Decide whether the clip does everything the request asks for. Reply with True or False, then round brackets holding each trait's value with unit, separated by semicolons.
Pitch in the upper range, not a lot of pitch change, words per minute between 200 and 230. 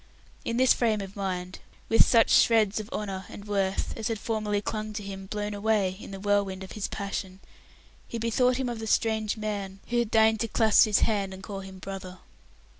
True (210 Hz; 2.3 semitones; 205 wpm)